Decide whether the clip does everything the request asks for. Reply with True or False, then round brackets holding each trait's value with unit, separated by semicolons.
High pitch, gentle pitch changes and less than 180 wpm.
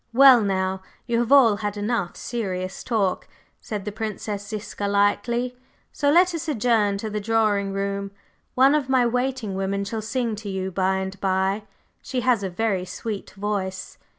False (210 Hz; 3.3 semitones; 170 wpm)